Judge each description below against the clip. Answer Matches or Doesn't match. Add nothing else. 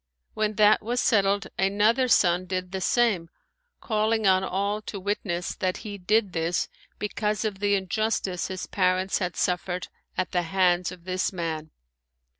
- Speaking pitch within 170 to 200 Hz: Matches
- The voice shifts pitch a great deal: Doesn't match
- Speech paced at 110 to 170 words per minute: Matches